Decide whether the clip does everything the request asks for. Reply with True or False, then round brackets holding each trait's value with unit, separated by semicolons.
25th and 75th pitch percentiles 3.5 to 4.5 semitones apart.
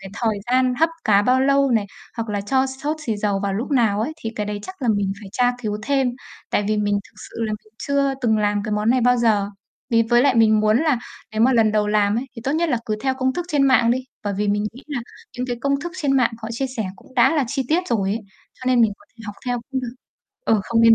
True (3.8 semitones)